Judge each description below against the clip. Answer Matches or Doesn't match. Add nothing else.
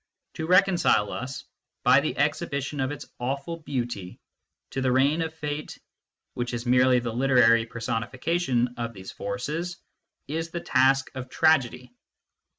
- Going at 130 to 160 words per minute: Matches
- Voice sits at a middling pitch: Doesn't match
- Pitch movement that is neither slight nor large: Matches